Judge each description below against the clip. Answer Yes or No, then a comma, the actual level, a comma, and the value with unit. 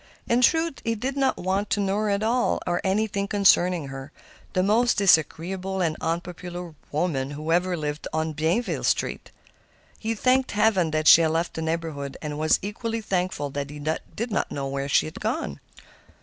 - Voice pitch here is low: No, medium, 180 Hz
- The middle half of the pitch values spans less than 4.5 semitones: No, average, 4.9 semitones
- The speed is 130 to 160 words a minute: No, average, 175 wpm